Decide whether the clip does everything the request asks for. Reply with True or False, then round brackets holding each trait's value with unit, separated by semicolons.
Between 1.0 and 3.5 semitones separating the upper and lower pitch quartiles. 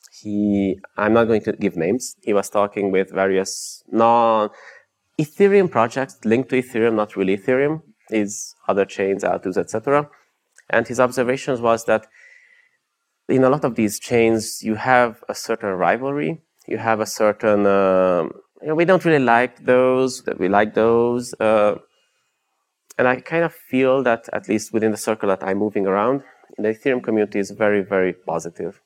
False (3.9 semitones)